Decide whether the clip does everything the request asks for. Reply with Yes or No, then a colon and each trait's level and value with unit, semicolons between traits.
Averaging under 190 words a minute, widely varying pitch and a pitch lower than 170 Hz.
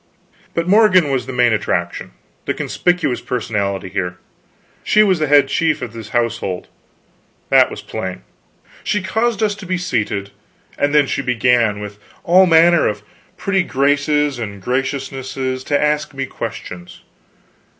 Yes: average, 140 wpm; wide, 7.3 semitones; low, 135 Hz